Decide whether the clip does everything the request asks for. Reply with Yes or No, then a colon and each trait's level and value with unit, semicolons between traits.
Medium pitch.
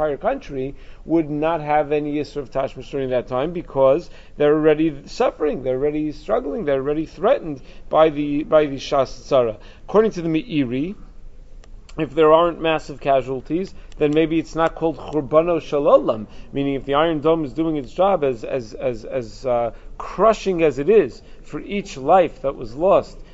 Yes: medium, 150 Hz